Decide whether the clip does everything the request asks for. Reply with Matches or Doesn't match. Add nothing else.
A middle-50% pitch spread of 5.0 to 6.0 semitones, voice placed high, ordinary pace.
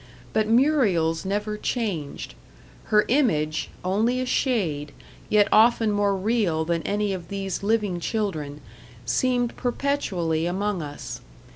Doesn't match